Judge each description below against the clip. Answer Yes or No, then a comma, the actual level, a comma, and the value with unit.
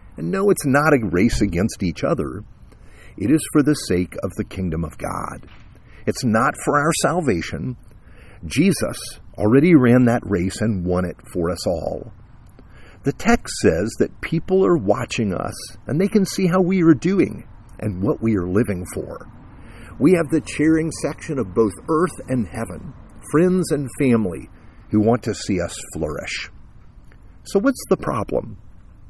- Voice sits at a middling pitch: No, low, 115 Hz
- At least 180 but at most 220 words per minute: No, average, 165 wpm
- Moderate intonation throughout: No, wide, 7.7 semitones